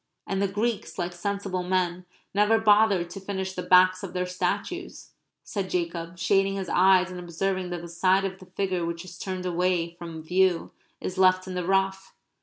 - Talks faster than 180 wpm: Yes, average, 190 wpm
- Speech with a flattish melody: Yes, narrow, 1.6 semitones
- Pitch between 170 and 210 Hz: Yes, medium, 185 Hz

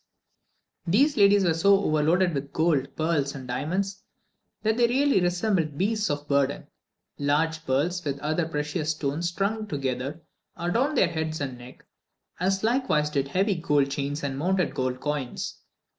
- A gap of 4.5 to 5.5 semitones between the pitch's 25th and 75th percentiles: Yes, average, 5.1 semitones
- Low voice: No, medium, 160 Hz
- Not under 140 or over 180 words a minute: Yes, average, 150 wpm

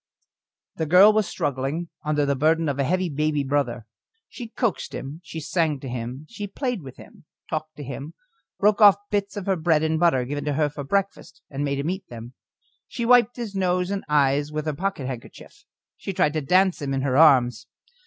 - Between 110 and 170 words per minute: No, fast, 205 wpm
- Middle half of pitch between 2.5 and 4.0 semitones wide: No, average, 5.1 semitones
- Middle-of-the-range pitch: Yes, medium, 155 Hz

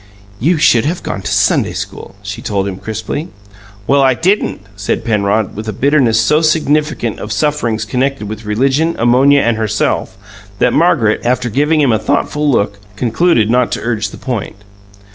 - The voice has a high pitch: No, low, 120 Hz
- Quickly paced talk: No, average, 170 wpm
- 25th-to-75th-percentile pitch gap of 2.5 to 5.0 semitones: No, wide, 5.4 semitones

